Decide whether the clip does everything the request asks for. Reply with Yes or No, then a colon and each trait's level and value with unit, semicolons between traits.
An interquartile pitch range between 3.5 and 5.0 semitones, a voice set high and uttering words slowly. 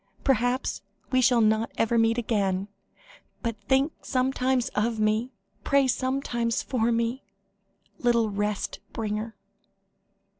No: average, 2.8 semitones; high, 235 Hz; slow, 110 wpm